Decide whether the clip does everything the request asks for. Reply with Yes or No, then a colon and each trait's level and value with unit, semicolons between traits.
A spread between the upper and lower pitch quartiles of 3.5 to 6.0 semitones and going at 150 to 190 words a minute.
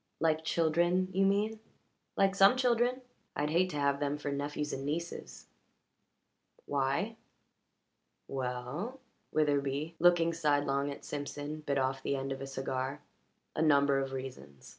No: average, 4.0 semitones; average, 140 wpm